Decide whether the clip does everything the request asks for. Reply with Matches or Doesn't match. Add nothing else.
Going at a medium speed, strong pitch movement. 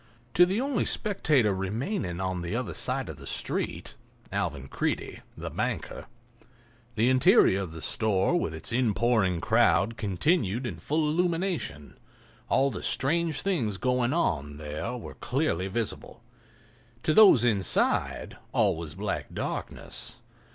Doesn't match